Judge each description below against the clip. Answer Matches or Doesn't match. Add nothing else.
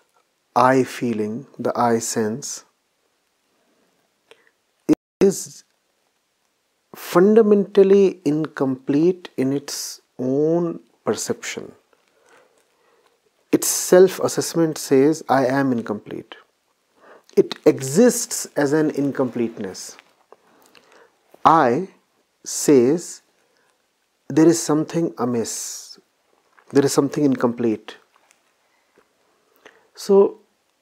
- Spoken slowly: Matches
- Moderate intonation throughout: Doesn't match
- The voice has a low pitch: Doesn't match